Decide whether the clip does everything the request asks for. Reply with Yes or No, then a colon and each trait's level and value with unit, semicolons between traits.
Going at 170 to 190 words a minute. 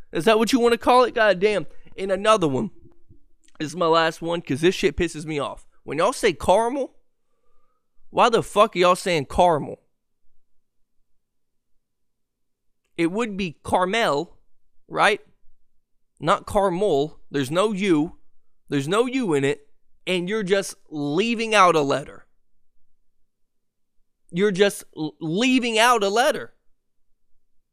No: average, 140 wpm